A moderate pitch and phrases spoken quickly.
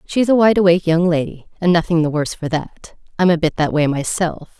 Yes: medium, 170 Hz; fast, 250 wpm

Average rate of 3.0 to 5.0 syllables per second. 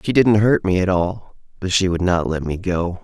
Yes: 4.8 syllables/s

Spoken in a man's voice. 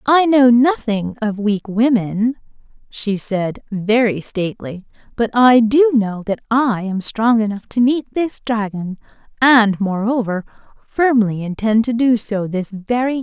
No: female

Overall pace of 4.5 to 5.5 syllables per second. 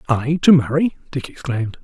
Yes: 5.4 syllables/s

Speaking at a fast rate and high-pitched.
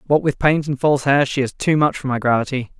No: fast, 280 wpm; medium, 140 Hz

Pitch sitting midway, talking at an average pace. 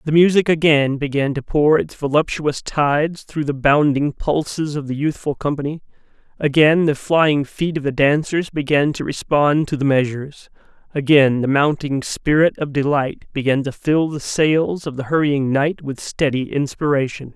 Yes: medium, 145 Hz; average, 165 wpm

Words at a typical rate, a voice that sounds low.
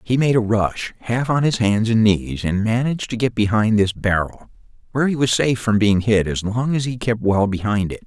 No: fast, 240 wpm; low, 110 Hz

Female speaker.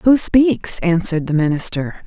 Yes: female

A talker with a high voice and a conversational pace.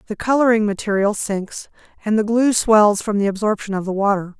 Yes: high, 210 Hz; average, 190 wpm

